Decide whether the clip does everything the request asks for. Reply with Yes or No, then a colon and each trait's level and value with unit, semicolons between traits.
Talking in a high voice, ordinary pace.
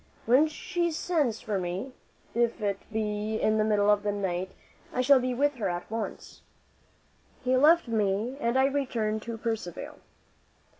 Yes: high, 225 Hz; average, 160 wpm